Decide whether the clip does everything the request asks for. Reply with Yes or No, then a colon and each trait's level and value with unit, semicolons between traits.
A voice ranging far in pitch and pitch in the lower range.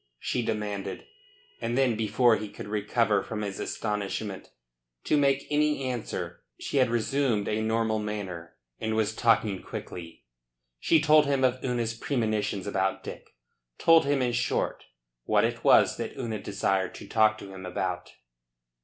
No: average, 3.6 semitones; low, 110 Hz